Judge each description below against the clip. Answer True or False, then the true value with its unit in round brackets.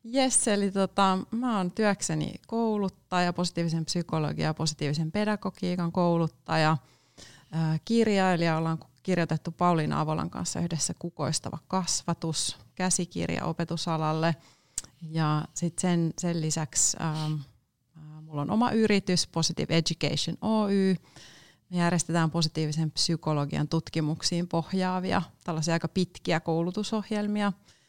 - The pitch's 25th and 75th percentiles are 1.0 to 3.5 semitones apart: True (2.9 semitones)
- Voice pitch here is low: False (165 Hz)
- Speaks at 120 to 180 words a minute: False (100 wpm)